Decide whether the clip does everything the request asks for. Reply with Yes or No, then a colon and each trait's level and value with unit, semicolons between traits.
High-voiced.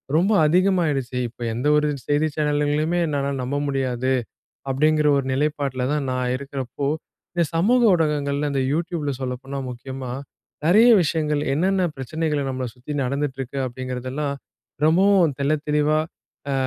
No: medium, 145 Hz